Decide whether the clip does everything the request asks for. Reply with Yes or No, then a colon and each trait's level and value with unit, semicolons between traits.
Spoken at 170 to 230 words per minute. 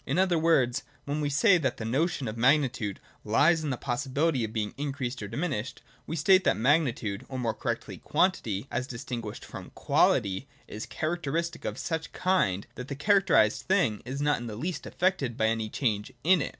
Yes: average, 190 wpm